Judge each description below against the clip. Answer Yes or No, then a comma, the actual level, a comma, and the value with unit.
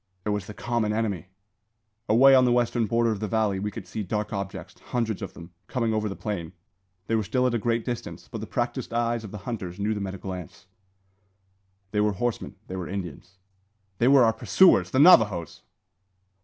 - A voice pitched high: No, low, 110 Hz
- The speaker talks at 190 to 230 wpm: Yes, fast, 205 wpm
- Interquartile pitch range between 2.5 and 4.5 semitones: Yes, average, 3.2 semitones